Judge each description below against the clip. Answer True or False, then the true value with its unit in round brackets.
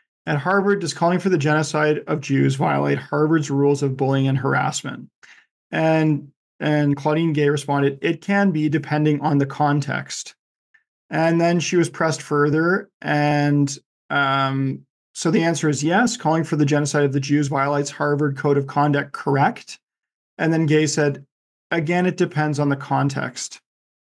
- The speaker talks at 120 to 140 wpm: False (160 wpm)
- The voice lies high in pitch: False (150 Hz)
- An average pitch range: False (2.3 semitones)